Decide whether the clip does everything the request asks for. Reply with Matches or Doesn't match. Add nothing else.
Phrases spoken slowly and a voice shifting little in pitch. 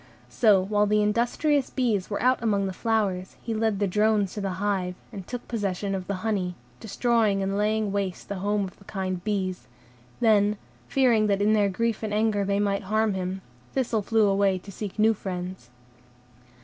Doesn't match